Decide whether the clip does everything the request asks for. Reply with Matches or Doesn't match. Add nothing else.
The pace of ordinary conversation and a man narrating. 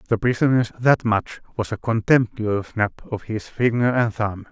Matches